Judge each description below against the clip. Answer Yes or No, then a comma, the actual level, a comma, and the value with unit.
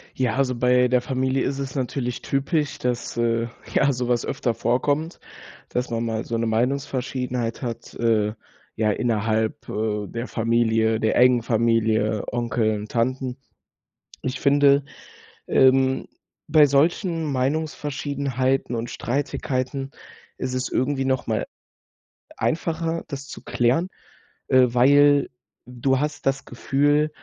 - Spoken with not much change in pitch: No, average, 3.0 semitones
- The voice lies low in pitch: Yes, low, 130 Hz